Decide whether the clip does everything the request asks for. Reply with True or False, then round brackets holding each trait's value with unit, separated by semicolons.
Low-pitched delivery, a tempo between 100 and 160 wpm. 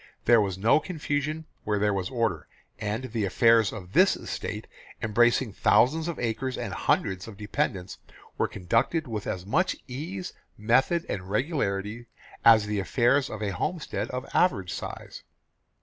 True (115 Hz; 150 wpm)